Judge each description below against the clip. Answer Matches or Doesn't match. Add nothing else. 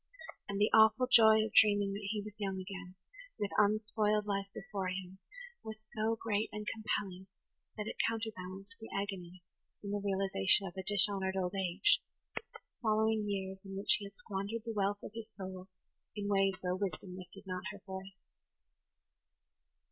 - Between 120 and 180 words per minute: Matches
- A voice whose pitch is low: Doesn't match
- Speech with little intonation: Matches